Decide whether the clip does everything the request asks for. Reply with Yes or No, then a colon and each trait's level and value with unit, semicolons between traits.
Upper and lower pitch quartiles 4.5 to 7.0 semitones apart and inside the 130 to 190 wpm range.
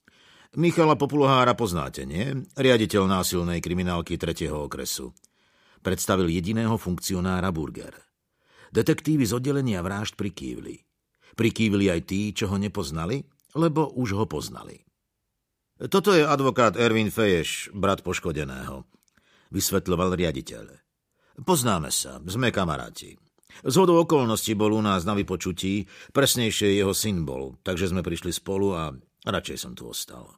No: average, 5.1 semitones; average, 120 wpm